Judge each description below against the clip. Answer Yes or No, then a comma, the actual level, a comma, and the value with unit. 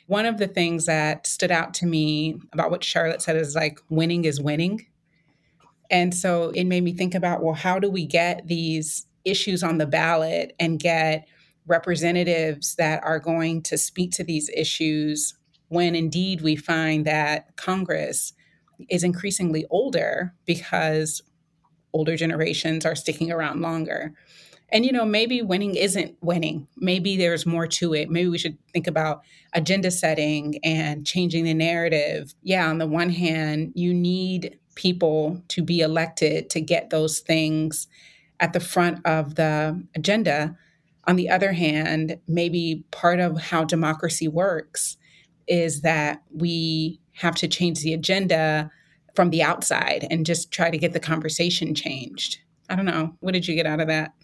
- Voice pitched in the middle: Yes, medium, 165 Hz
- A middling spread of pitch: No, narrow, 1.8 semitones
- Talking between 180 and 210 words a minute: No, average, 160 wpm